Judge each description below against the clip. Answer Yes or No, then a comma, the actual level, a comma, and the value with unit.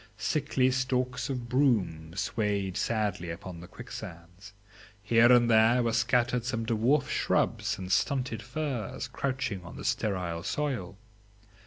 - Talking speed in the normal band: No, slow, 130 wpm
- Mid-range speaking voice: No, low, 115 Hz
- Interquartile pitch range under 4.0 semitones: No, average, 5.0 semitones